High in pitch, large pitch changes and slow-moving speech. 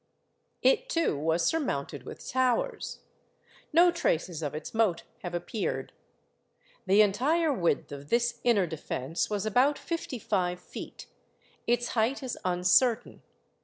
Yes: high, 220 Hz; wide, 6.9 semitones; slow, 130 wpm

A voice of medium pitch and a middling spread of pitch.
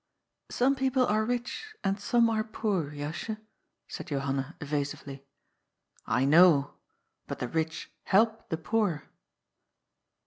No: medium, 180 Hz; wide, 7.6 semitones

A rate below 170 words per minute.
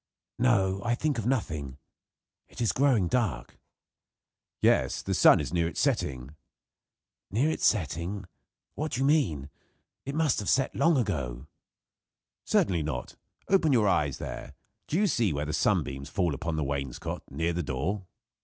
Yes: average, 155 wpm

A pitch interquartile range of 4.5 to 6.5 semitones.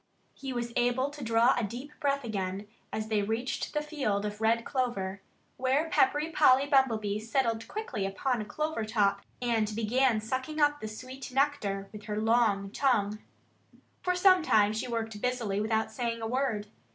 No: average, 4.0 semitones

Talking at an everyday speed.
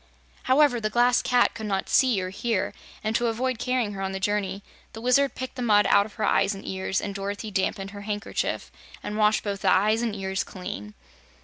No: fast, 215 wpm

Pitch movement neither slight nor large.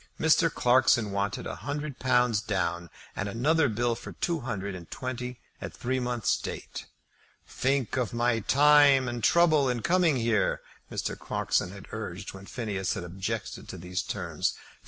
Yes: average, 4.8 semitones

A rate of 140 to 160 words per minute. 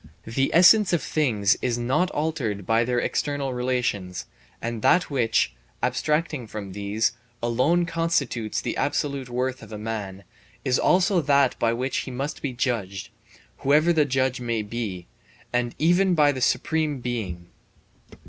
Yes: average, 145 wpm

